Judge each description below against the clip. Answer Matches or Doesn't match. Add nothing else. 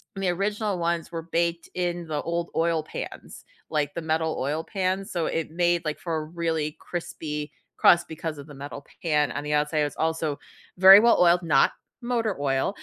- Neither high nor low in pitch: Matches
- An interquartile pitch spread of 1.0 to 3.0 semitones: Matches